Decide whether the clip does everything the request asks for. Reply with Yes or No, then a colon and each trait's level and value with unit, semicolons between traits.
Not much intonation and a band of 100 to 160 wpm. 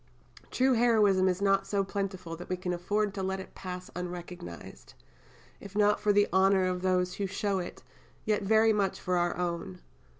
No: narrow, 2.2 semitones; average, 180 wpm